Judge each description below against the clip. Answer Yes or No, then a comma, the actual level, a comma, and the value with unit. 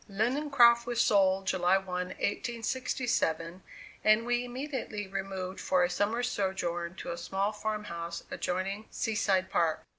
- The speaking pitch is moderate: No, high, 195 Hz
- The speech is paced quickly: No, average, 140 wpm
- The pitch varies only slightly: No, average, 4.2 semitones